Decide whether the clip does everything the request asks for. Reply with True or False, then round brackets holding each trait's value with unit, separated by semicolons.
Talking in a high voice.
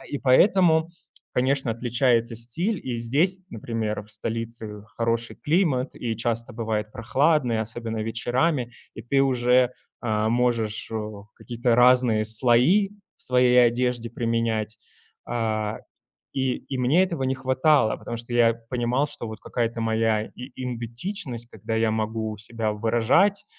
False (120 Hz)